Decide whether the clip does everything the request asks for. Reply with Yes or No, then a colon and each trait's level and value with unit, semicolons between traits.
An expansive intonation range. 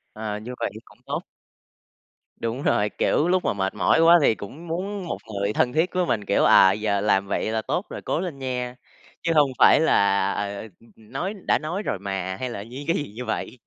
Yes: wide, 7.5 semitones